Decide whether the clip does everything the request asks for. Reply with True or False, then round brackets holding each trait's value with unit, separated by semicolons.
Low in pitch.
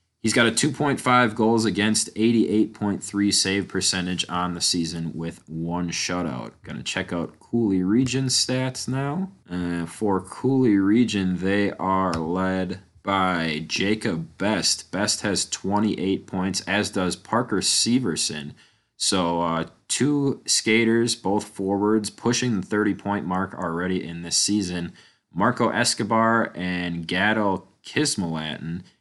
True (100 Hz)